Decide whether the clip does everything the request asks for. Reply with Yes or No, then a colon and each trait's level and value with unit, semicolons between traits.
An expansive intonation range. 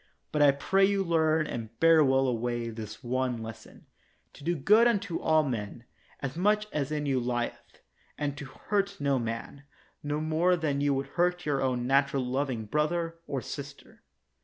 No: average, 4.3 semitones